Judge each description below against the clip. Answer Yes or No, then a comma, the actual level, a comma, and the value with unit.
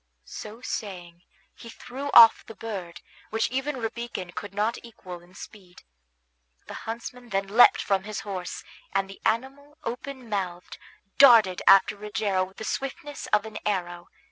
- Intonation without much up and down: No, average, 3.8 semitones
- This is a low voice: No, high, 210 Hz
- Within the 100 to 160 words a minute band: Yes, average, 150 wpm